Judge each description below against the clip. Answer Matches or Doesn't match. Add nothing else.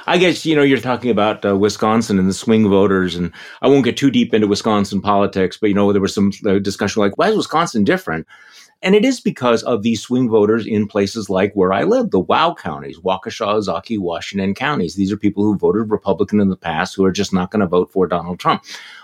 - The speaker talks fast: Matches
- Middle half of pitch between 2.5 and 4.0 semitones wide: Matches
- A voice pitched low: Matches